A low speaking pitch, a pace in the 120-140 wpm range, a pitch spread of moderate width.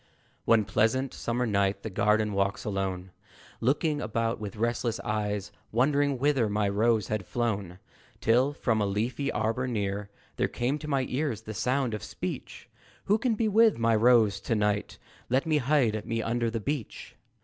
No: low, 115 Hz; average, 165 wpm; average, 3.8 semitones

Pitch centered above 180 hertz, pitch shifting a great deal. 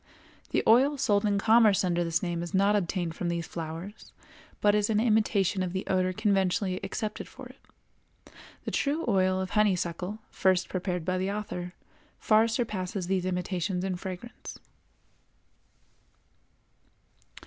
No: high, 190 Hz; average, 2.8 semitones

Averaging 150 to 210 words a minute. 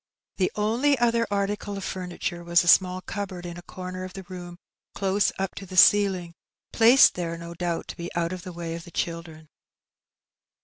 Yes: average, 190 wpm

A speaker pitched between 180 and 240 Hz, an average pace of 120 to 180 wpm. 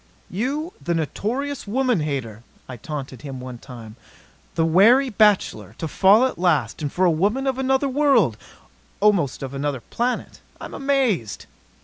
Yes: medium, 185 Hz; average, 150 wpm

